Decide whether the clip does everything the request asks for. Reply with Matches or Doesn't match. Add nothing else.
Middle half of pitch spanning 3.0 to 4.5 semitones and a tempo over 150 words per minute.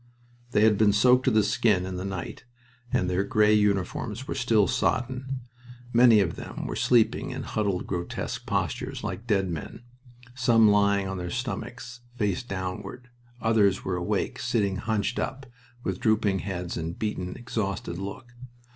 Matches